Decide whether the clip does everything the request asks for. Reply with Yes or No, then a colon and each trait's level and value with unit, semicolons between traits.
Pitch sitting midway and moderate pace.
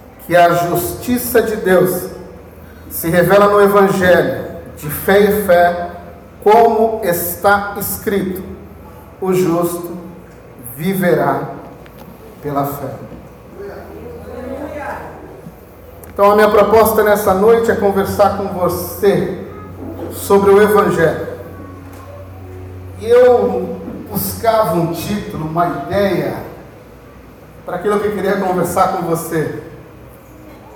No: medium, 180 Hz; slow, 95 wpm